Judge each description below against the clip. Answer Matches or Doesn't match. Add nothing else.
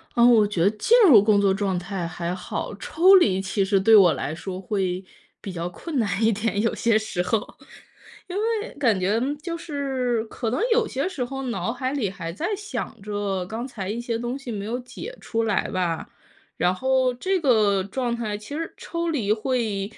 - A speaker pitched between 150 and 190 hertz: Doesn't match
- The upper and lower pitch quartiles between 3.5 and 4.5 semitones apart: Doesn't match